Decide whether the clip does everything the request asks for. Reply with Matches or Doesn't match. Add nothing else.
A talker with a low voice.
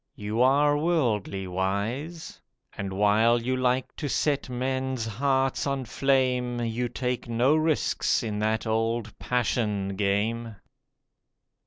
Matches